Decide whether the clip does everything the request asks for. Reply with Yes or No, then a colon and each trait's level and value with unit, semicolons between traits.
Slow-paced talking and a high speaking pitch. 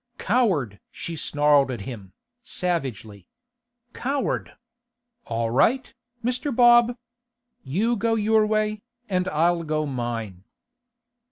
No: slow, 100 wpm; medium, 170 Hz